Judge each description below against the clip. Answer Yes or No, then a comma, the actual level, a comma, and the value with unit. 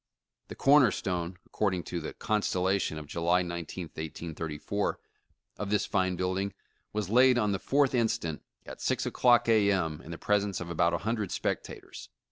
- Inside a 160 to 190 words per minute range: Yes, average, 175 wpm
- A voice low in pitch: Yes, very low, 95 Hz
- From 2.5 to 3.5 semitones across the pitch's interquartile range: No, average, 3.9 semitones